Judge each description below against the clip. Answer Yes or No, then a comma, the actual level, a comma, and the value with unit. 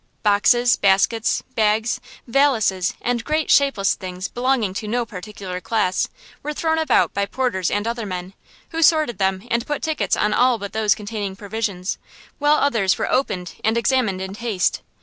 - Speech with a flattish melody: No, average, 4.2 semitones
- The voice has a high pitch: Yes, high, 220 Hz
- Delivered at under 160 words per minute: No, average, 165 wpm